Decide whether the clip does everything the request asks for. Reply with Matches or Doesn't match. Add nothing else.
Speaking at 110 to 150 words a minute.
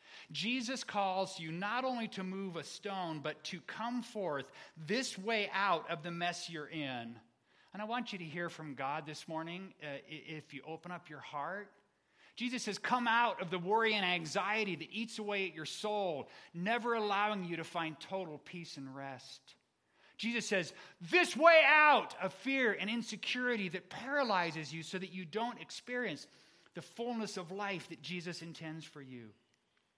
Doesn't match